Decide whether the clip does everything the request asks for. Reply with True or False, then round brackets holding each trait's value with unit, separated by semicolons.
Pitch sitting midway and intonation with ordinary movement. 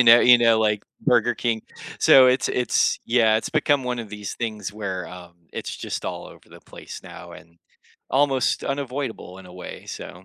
False (115 Hz; 3.4 semitones)